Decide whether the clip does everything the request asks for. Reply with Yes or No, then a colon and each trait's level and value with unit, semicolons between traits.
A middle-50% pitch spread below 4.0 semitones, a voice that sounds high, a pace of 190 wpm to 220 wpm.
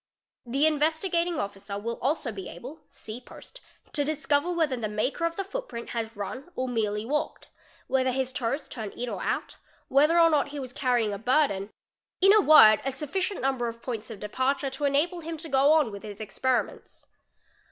No: average, 5.2 semitones; very high, 265 Hz; average, 195 wpm